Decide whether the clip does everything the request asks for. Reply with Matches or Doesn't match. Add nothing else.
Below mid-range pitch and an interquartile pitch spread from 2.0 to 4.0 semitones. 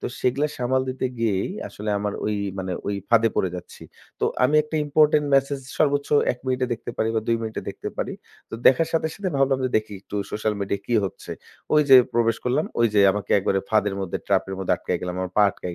Doesn't match